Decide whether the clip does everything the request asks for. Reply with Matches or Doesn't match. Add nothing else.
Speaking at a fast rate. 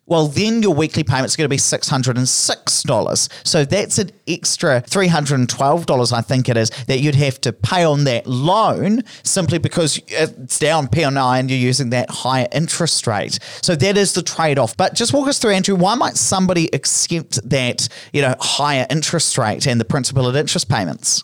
Doesn't match